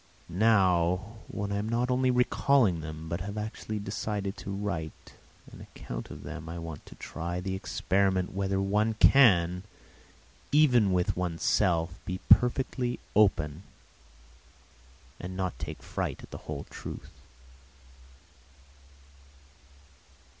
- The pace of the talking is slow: Yes, slow, 120 wpm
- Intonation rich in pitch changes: No, average, 4.0 semitones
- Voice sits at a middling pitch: No, very low, 95 Hz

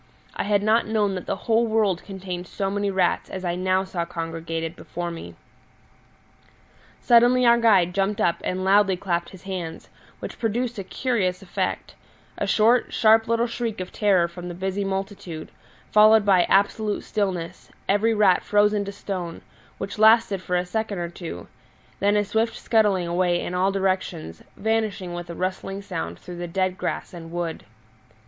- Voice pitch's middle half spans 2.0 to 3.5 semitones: Yes, average, 3.1 semitones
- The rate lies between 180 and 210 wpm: No, average, 170 wpm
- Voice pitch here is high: Yes, high, 195 Hz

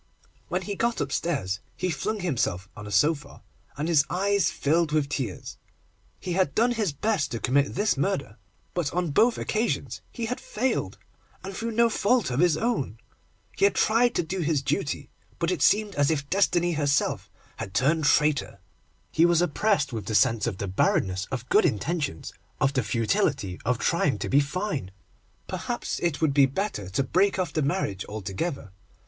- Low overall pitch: No, medium, 150 Hz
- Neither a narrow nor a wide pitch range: No, wide, 6.7 semitones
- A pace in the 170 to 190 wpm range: Yes, average, 180 wpm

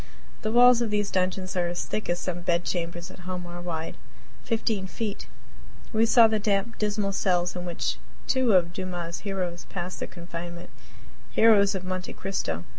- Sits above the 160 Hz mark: Yes, medium, 185 Hz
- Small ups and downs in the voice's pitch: No, average, 3.1 semitones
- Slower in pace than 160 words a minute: No, average, 175 wpm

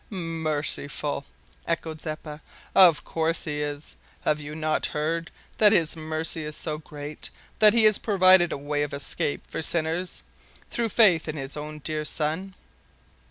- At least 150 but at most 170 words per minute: Yes, average, 155 wpm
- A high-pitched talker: No, medium, 155 Hz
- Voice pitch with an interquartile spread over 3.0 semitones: No, narrow, 2.4 semitones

